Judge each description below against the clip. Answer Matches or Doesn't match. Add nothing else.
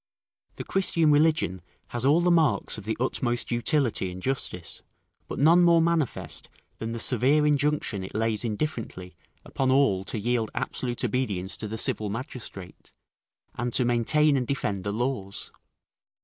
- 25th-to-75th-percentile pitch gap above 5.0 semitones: Matches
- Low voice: Matches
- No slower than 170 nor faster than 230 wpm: Doesn't match